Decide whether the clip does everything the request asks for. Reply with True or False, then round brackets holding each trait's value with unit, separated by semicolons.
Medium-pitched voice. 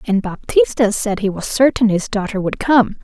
False (220 Hz)